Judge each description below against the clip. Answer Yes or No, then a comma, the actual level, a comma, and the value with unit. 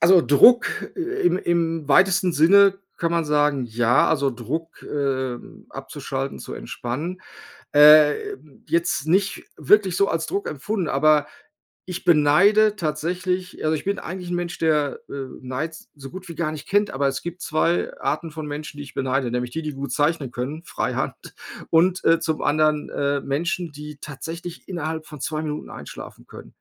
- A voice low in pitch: No, medium, 155 Hz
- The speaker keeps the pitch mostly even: No, average, 3.4 semitones